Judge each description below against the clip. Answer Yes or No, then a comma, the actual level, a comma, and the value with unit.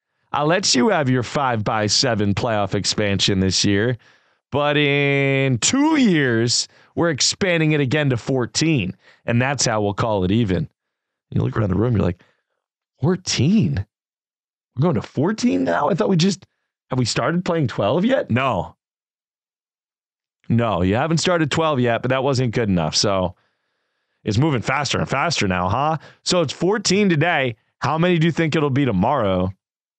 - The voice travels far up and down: Yes, wide, 6.5 semitones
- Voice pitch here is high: No, low, 130 Hz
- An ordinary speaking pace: Yes, average, 170 wpm